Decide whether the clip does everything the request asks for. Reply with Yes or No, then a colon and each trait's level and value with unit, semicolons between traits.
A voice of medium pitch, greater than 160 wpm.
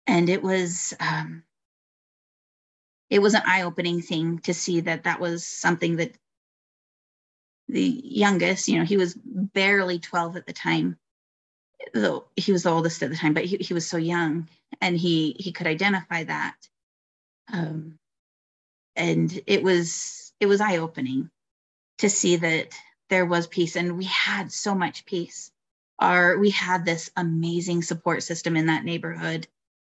No: medium, 175 Hz; average, 155 wpm